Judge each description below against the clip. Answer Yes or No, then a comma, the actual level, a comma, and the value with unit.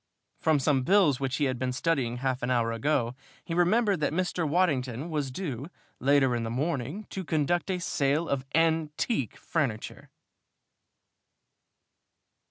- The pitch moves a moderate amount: Yes, average, 4.5 semitones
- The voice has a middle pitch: Yes, medium, 145 Hz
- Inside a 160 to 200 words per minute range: No, average, 145 wpm